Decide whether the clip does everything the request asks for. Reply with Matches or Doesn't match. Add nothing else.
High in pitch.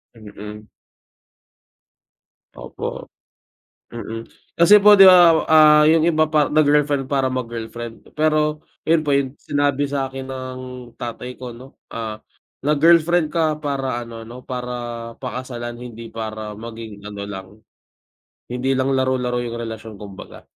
Doesn't match